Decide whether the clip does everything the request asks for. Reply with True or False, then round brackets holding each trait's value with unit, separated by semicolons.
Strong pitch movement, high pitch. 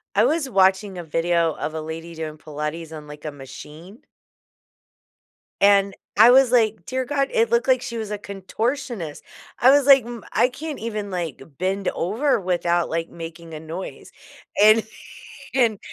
True (6.5 semitones; 195 Hz)